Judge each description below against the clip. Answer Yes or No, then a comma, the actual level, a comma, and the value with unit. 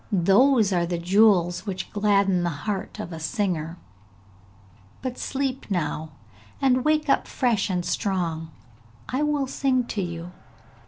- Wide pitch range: Yes, wide, 6.4 semitones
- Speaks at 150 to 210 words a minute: No, average, 140 wpm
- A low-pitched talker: No, high, 195 Hz